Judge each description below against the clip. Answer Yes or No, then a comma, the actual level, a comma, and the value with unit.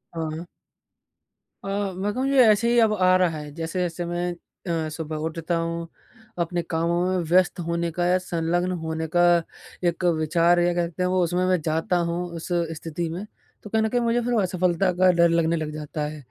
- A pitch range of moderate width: No, narrow, 2.1 semitones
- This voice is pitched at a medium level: Yes, medium, 175 Hz